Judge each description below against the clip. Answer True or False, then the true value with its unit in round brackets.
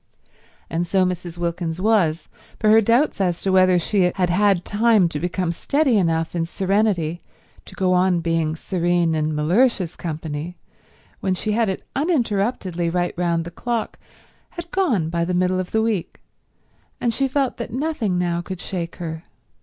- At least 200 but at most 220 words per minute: False (170 wpm)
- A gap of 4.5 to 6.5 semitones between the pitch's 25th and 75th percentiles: False (4.1 semitones)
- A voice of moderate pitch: True (180 Hz)